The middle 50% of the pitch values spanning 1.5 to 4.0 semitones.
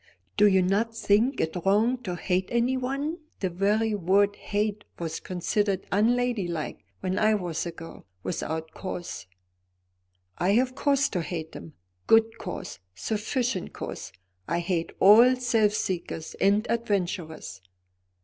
No: average, 4.5 semitones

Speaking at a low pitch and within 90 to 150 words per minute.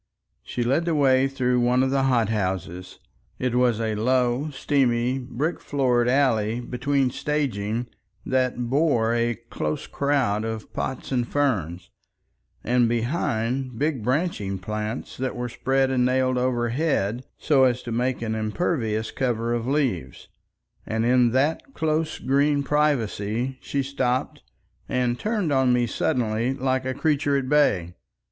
Yes: low, 125 Hz; average, 140 wpm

